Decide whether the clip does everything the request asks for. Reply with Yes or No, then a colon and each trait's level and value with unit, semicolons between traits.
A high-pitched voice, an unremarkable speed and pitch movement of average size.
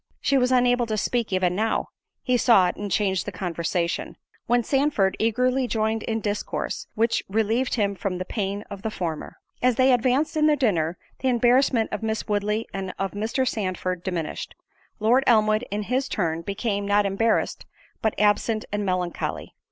Yes: high, 215 Hz; average, 170 wpm; average, 3.9 semitones